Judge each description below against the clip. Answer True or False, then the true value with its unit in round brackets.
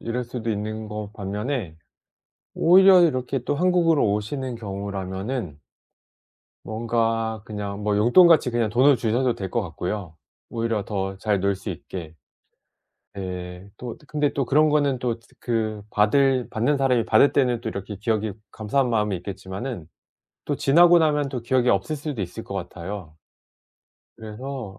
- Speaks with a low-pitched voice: True (115 Hz)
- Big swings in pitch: False (4.8 semitones)